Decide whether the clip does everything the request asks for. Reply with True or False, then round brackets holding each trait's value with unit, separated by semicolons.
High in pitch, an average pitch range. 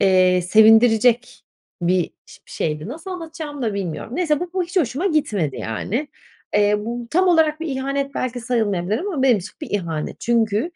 False (240 Hz; 7.3 semitones)